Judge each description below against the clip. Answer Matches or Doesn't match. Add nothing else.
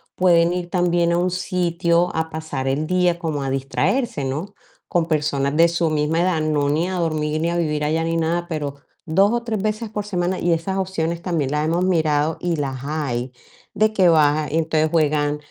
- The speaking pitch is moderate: Matches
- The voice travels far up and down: Doesn't match